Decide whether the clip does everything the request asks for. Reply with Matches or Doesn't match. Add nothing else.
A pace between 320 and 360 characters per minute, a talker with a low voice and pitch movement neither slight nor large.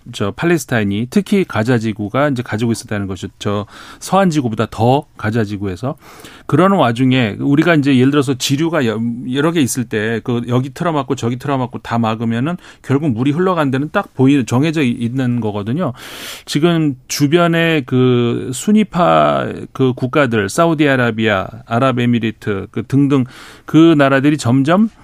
Matches